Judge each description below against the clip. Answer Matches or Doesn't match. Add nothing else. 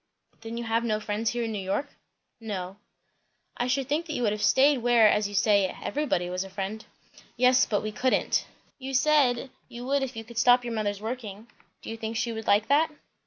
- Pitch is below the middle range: Doesn't match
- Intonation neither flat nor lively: Matches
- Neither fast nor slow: Doesn't match